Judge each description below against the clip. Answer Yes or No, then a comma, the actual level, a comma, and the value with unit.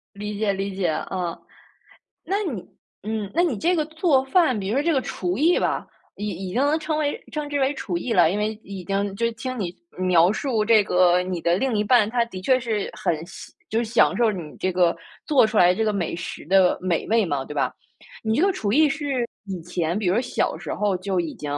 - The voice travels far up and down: Yes, wide, 5.9 semitones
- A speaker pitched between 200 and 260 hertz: Yes, high, 210 Hz